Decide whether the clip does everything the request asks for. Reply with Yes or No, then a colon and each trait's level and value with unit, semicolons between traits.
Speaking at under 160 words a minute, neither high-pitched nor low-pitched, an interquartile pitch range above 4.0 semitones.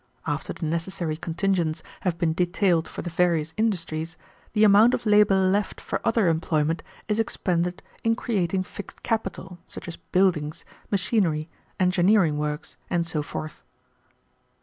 No: average, 140 wpm; medium, 180 Hz; average, 3.3 semitones